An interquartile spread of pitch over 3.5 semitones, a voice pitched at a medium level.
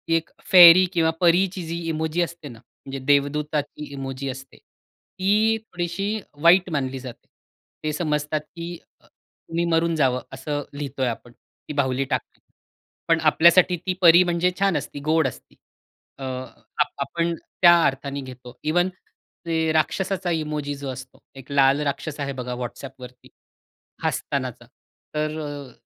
Yes: average, 3.9 semitones; medium, 150 Hz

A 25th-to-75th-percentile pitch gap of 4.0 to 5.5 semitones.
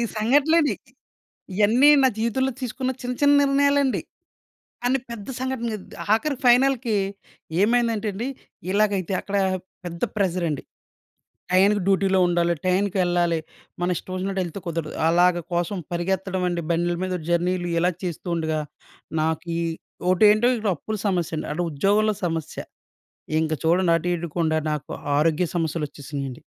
Yes: average, 4.7 semitones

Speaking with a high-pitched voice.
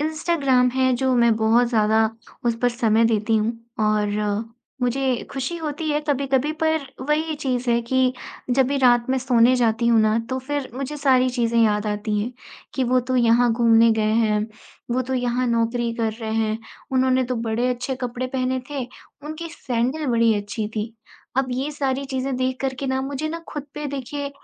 Yes: very high, 250 Hz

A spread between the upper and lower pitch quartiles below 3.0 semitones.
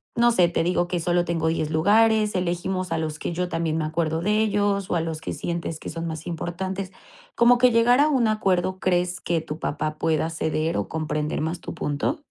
No: average, 3.6 semitones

